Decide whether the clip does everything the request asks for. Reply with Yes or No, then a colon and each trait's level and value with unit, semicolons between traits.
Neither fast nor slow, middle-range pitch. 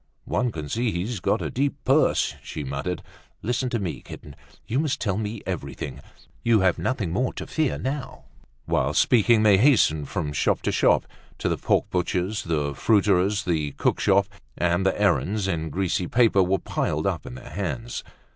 No: average, 175 wpm; very low, 95 Hz